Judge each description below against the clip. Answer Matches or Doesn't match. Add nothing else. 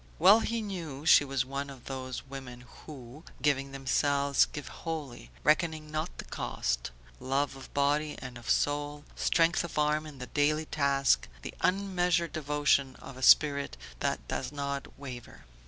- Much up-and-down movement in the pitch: Doesn't match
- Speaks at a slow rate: Doesn't match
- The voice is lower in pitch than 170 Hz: Matches